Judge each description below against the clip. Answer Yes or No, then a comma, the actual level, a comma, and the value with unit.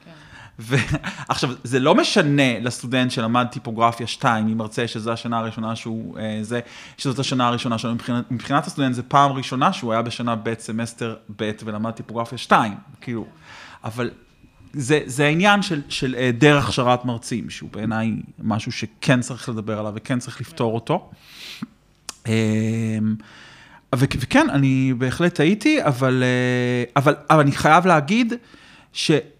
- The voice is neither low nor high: No, low, 125 Hz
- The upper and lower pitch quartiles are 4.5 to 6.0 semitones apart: No, average, 3.6 semitones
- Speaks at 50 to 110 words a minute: No, average, 135 wpm